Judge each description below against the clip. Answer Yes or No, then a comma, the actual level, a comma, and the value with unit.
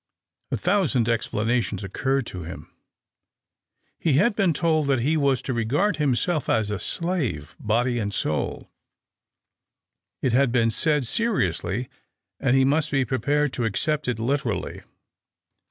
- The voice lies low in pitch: Yes, low, 130 Hz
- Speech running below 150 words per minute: Yes, average, 140 wpm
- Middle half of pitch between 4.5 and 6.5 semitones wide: Yes, average, 5.0 semitones